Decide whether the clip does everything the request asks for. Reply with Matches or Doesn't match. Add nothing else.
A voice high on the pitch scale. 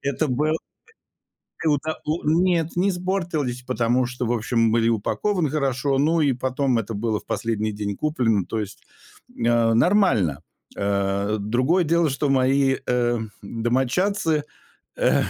Doesn't match